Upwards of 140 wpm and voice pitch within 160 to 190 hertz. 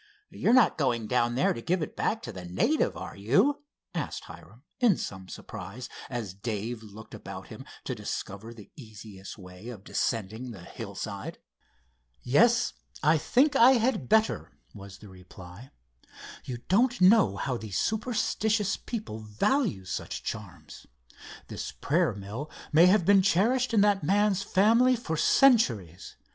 No: average, 150 wpm; low, 130 Hz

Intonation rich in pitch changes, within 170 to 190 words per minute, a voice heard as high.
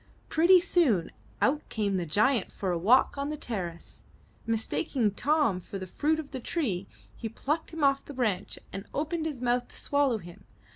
Yes: wide, 6.9 semitones; average, 185 wpm; very high, 250 Hz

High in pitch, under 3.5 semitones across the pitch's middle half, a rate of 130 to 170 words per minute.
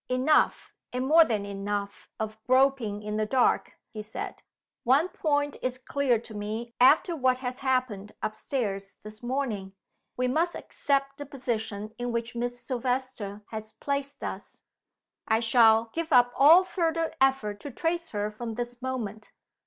No: high, 245 Hz; average, 4.0 semitones; average, 155 wpm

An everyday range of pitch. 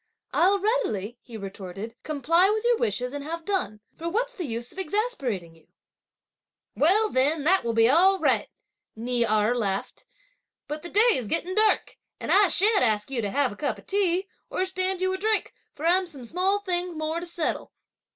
No: wide, 8.2 semitones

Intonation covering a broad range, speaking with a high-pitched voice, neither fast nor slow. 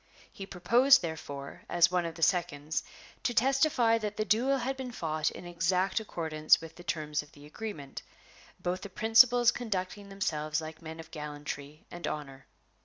No: wide, 6.2 semitones; medium, 175 Hz; average, 170 wpm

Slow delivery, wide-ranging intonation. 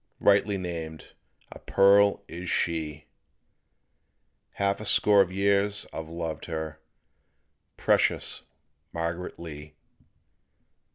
No: slow, 95 wpm; average, 3.7 semitones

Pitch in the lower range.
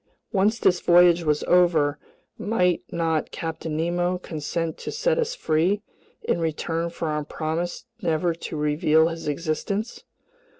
No: medium, 170 Hz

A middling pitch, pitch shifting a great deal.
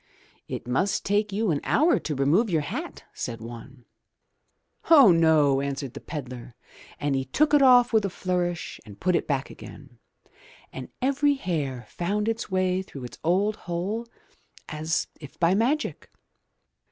Yes: medium, 170 Hz; wide, 7.3 semitones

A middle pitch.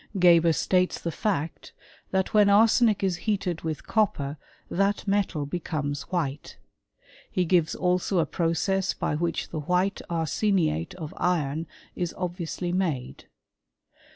Yes: medium, 175 Hz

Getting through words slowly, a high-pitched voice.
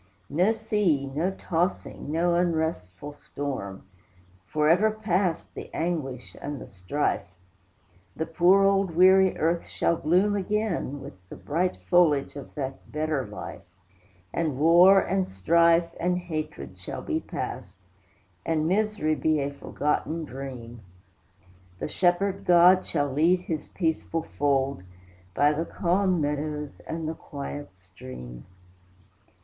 No: slow, 125 wpm; medium, 160 Hz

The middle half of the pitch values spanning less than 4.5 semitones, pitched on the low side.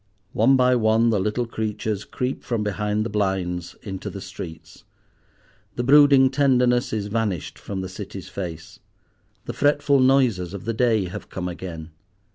No: average, 4.8 semitones; low, 110 Hz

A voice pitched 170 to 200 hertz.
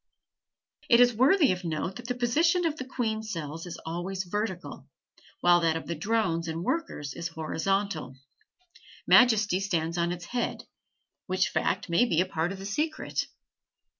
Yes: high, 190 Hz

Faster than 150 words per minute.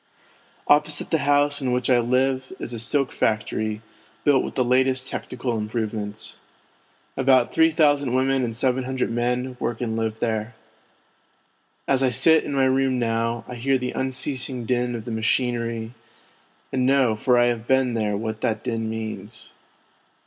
Yes: average, 170 wpm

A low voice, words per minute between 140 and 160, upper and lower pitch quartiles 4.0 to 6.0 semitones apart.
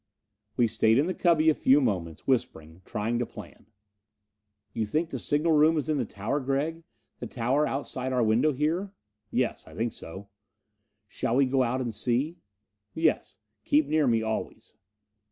No: low, 130 Hz; average, 170 wpm; average, 5.0 semitones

